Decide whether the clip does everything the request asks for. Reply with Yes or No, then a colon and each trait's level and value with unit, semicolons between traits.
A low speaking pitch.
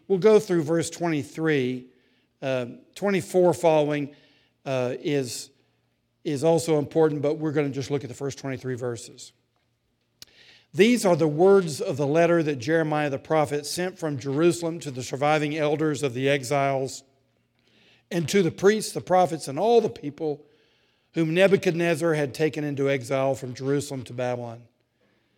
No: medium, 145 Hz